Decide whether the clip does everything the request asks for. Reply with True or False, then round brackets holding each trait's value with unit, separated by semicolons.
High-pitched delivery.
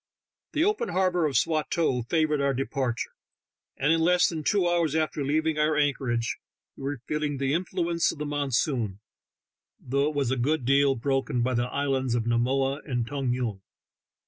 False (140 Hz)